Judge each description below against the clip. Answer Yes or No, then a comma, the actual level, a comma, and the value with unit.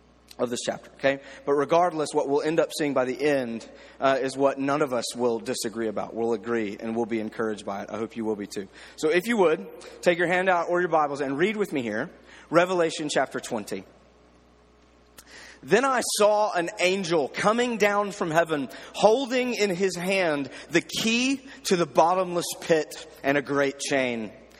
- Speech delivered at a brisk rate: No, average, 195 wpm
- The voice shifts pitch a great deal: Yes, wide, 7.4 semitones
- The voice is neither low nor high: Yes, medium, 145 Hz